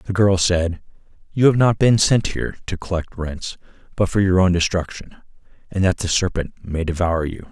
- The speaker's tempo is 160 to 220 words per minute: Yes, average, 190 wpm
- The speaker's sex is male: Yes, male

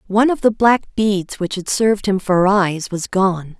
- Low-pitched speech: No, high, 200 Hz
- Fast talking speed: Yes, fast, 215 wpm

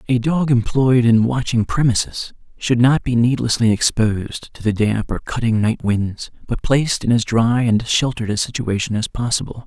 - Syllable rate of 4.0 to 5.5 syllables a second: Yes, 5.0 syllables/s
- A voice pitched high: No, low, 120 Hz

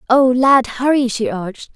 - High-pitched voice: Yes, high, 245 Hz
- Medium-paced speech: Yes, average, 170 wpm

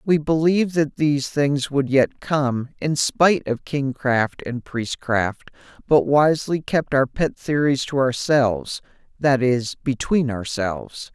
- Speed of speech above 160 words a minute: No, average, 140 wpm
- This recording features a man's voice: Yes, male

